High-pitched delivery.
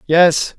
No: medium, 165 Hz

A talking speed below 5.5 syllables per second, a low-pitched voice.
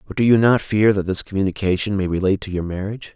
No: 7.0 syllables/s; low, 100 Hz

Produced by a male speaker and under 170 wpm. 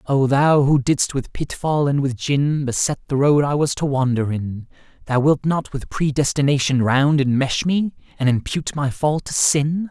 No: male; average, 190 wpm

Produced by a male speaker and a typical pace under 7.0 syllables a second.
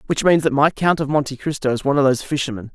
No: male; 7.3 syllables/s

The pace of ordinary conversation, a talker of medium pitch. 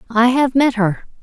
No: average, 195 wpm; high, 240 Hz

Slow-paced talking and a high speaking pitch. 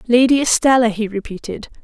Yes: slow, 130 wpm; high, 235 Hz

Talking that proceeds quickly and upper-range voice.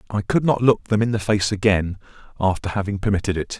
No: fast, 215 wpm; low, 105 Hz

